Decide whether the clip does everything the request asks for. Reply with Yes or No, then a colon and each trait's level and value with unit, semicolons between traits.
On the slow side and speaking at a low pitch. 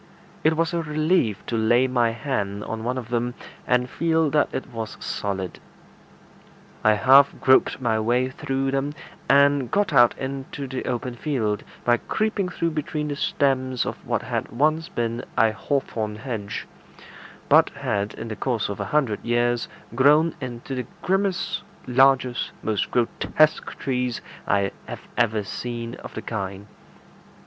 No: average, 155 wpm; low, 125 Hz